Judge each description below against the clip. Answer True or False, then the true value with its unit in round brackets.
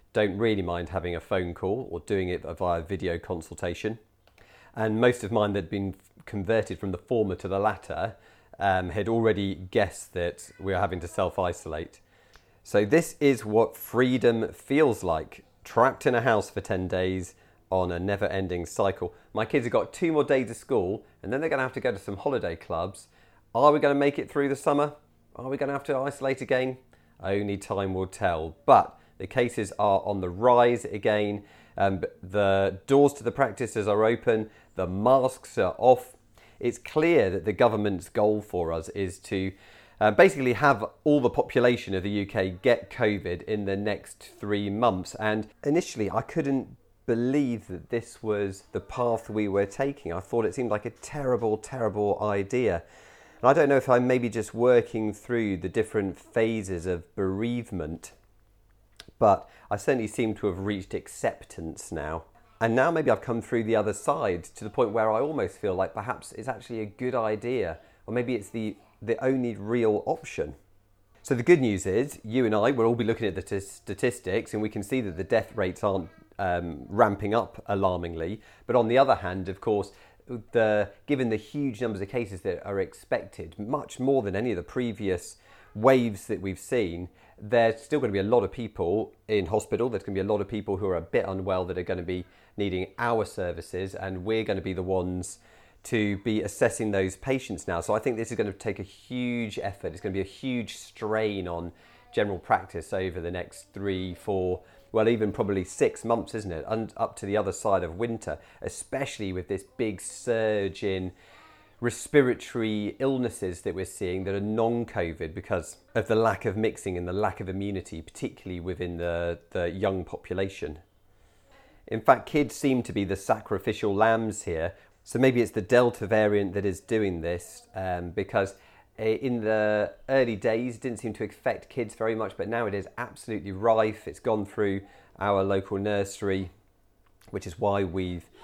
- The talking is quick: False (190 wpm)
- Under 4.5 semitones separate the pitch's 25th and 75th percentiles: True (3.6 semitones)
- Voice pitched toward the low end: True (105 Hz)